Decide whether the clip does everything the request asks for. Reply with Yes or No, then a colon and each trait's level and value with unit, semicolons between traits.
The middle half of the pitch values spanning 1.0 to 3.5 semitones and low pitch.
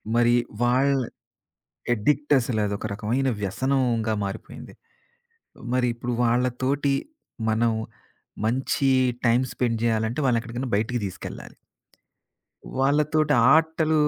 Yes: average, 3.0 semitones; low, 125 Hz